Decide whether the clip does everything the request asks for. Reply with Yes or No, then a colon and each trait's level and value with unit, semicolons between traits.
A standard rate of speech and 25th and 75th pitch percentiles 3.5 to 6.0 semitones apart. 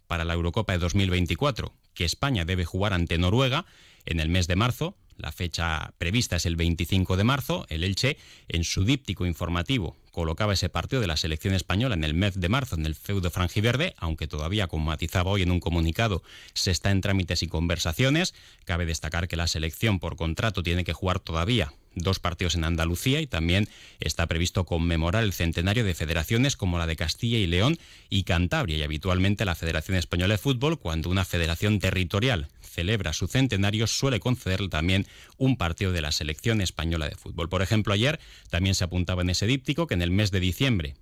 No: fast, 195 wpm; average, 3.8 semitones